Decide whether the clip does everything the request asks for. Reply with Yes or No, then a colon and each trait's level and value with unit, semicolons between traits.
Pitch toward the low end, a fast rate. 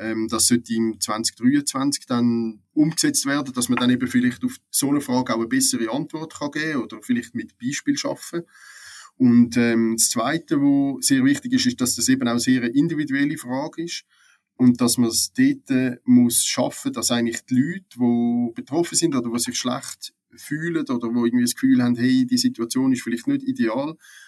No: medium, 155 Hz; fast, 200 wpm